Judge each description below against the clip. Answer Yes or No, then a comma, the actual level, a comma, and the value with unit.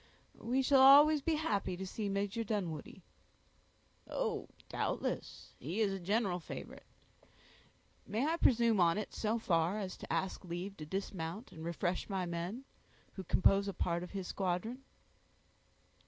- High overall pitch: Yes, high, 195 Hz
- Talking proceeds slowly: No, average, 150 wpm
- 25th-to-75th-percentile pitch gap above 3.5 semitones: Yes, average, 4.4 semitones